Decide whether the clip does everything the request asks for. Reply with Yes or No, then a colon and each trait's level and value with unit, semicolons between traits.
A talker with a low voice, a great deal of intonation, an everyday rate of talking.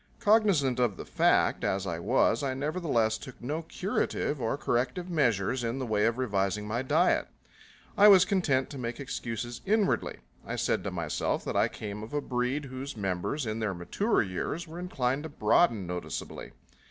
Yes: low, 125 Hz; wide, 5.8 semitones; average, 175 wpm